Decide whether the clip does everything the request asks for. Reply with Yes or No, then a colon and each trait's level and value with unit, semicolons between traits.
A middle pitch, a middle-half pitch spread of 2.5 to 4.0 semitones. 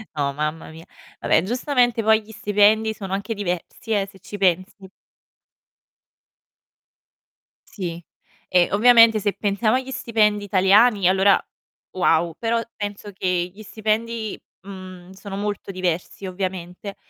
No: high, 200 Hz; average, 2.8 semitones